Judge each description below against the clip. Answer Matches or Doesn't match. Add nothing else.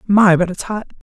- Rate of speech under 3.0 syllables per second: Doesn't match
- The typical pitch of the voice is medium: Doesn't match